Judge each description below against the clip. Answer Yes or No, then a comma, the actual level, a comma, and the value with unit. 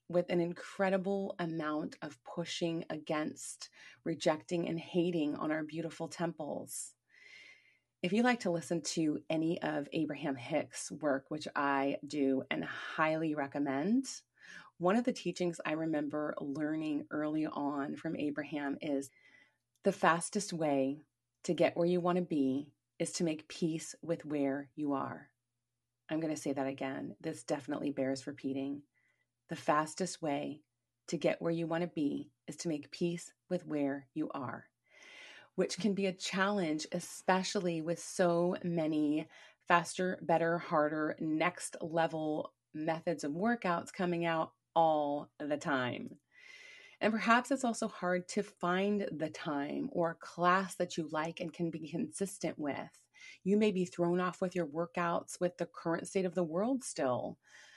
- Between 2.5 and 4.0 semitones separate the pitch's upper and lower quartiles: Yes, average, 3.2 semitones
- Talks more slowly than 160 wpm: Yes, average, 150 wpm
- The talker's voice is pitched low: No, medium, 165 Hz